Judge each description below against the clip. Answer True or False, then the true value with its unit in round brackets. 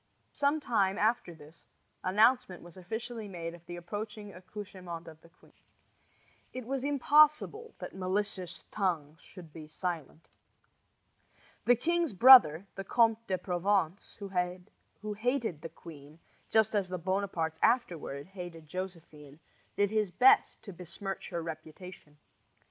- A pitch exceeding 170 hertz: True (185 Hz)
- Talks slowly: True (130 wpm)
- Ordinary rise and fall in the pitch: True (4.5 semitones)